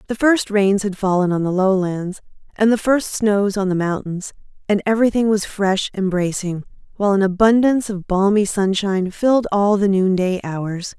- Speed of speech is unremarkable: Yes, average, 175 wpm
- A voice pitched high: Yes, high, 200 Hz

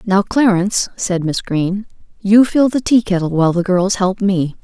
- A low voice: No, high, 195 Hz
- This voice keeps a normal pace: Yes, average, 180 wpm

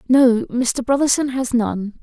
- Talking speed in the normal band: Yes, average, 150 wpm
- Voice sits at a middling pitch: No, very high, 250 Hz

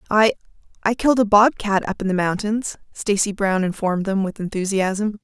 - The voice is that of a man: No, female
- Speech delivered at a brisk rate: No, average, 160 wpm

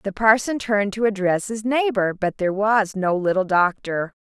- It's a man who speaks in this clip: No, female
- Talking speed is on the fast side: No, average, 185 wpm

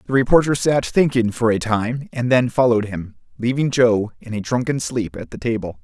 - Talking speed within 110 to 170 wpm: No, fast, 205 wpm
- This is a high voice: No, low, 120 Hz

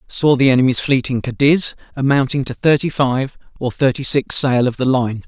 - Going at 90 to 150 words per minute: No, average, 195 wpm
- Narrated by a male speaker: Yes, male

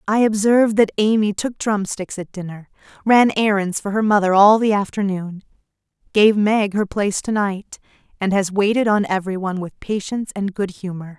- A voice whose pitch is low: No, high, 200 Hz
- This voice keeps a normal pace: Yes, average, 170 wpm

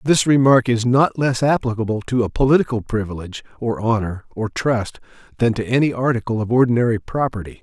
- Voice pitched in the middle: No, low, 120 Hz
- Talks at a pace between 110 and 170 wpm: Yes, average, 165 wpm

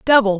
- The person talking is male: No, female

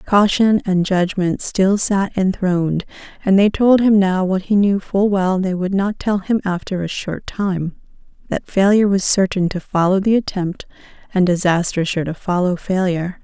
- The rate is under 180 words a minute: Yes, average, 170 wpm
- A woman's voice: Yes, female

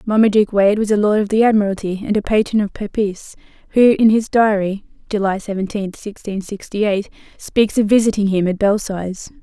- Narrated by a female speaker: Yes, female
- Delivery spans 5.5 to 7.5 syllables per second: No, 4.7 syllables/s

